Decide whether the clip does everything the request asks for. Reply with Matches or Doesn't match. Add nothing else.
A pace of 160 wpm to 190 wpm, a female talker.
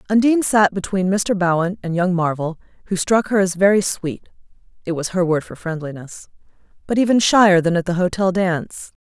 Matches